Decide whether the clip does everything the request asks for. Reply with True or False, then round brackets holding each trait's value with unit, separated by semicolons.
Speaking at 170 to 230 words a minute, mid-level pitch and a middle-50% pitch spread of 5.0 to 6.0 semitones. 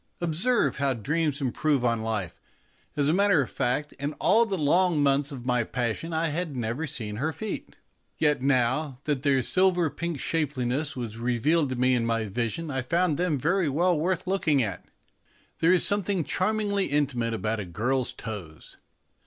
True (180 wpm; 145 Hz; 5.5 semitones)